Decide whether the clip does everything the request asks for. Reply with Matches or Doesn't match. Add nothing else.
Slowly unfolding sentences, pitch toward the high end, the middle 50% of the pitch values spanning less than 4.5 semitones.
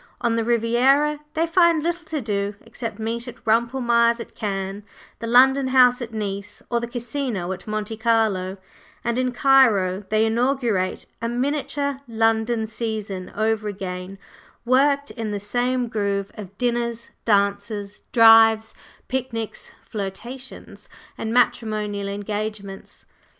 Matches